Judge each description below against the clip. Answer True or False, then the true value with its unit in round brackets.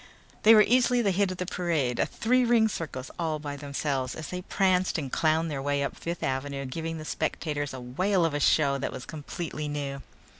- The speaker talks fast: True (215 wpm)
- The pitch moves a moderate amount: True (4.5 semitones)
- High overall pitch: False (155 Hz)